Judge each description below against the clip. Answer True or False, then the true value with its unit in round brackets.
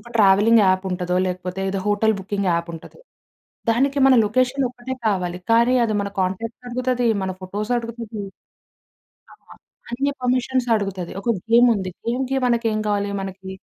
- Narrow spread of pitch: False (4.2 semitones)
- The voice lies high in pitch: True (220 Hz)